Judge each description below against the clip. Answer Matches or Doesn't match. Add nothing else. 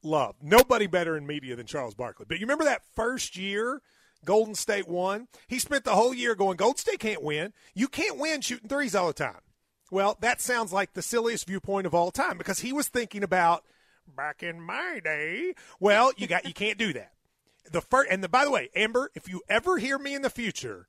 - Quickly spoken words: Matches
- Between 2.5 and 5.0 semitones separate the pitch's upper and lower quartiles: Doesn't match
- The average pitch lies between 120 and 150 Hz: Doesn't match